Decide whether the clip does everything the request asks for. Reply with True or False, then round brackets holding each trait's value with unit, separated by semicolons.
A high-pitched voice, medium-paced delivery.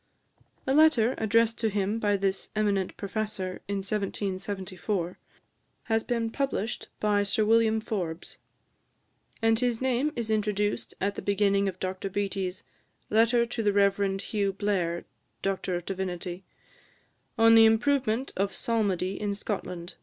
False (205 Hz; 130 wpm)